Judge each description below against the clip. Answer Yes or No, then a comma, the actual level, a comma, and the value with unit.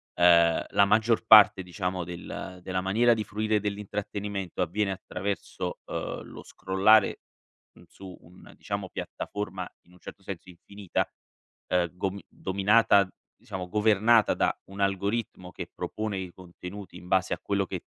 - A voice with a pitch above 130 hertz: No, very low, 95 Hz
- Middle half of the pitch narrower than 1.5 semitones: No, narrow, 2.4 semitones